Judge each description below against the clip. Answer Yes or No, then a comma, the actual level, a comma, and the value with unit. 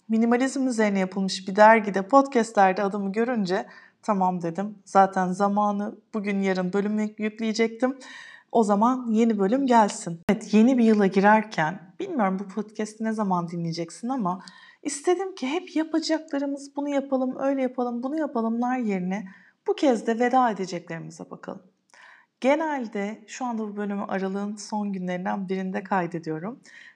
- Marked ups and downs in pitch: No, average, 4.8 semitones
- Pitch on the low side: No, high, 215 Hz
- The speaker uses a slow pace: No, average, 135 wpm